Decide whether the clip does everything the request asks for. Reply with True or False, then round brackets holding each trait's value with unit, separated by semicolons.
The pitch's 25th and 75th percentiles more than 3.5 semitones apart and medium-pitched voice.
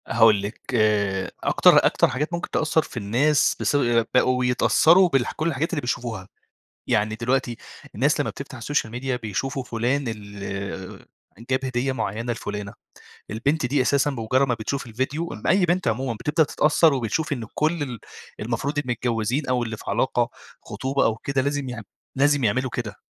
False (4.1 semitones; 125 Hz)